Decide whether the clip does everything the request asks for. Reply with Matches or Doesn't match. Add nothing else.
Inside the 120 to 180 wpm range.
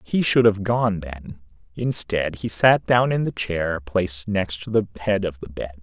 Doesn't match